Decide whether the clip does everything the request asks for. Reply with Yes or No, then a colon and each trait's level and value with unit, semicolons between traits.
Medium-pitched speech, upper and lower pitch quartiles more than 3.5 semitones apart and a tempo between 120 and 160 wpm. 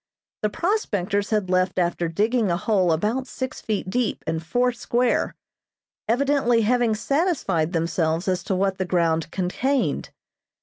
No: high, 205 Hz; wide, 5.6 semitones; average, 140 wpm